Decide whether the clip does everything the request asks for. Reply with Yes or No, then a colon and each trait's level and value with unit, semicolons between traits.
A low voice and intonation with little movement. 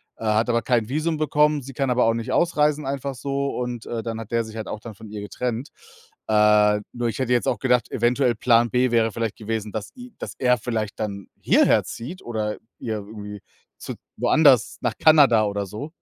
No: low, 115 Hz; average, 3.6 semitones